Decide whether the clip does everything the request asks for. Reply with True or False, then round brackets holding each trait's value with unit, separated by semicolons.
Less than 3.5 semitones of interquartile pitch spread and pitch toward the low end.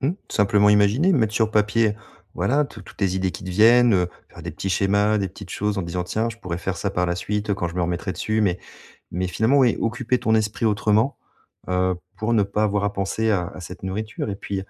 True (2.8 semitones; 105 Hz)